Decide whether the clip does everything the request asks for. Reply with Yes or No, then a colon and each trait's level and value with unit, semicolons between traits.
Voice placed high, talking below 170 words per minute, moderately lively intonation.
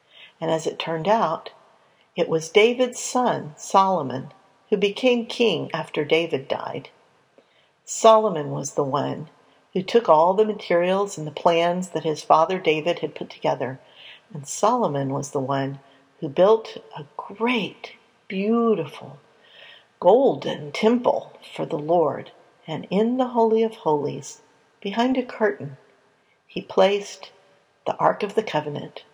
No: high, 195 Hz; slow, 135 wpm; wide, 6.2 semitones